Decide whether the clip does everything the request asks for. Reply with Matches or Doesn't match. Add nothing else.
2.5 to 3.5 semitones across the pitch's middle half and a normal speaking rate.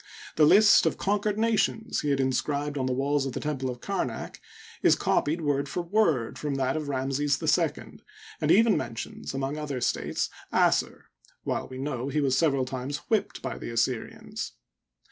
Matches